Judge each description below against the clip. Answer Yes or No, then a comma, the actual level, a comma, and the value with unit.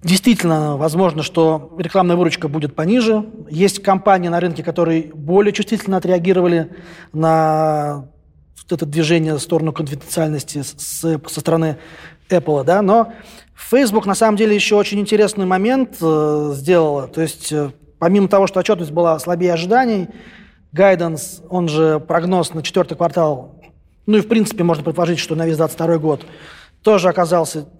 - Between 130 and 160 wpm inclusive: Yes, average, 140 wpm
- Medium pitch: Yes, medium, 170 Hz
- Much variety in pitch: No, average, 3.5 semitones